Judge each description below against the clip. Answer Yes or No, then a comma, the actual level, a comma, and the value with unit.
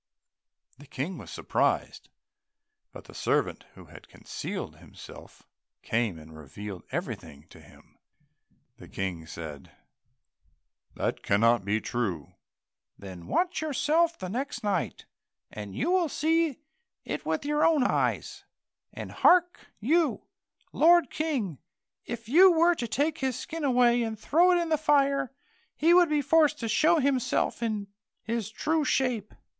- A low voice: No, very high, 260 Hz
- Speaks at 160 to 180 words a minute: No, average, 140 wpm